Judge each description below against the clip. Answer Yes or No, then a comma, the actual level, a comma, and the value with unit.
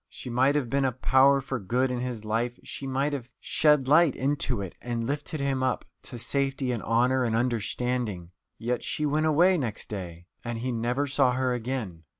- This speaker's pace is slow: No, average, 195 wpm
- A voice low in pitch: Yes, low, 125 Hz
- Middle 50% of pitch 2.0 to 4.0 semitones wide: Yes, average, 2.9 semitones